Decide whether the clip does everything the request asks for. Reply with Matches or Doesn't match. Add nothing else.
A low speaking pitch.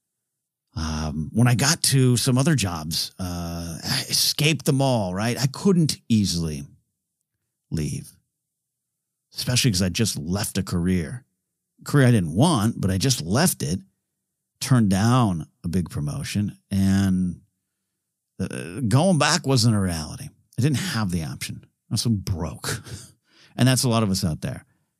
Matches